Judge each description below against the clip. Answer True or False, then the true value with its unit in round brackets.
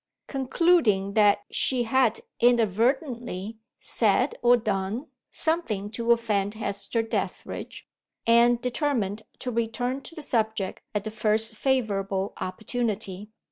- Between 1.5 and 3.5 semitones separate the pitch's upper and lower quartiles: True (3.2 semitones)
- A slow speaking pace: True (110 wpm)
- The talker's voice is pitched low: False (225 Hz)